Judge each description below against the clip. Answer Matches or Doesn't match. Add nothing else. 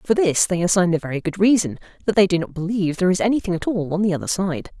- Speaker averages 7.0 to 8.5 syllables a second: Matches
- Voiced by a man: Doesn't match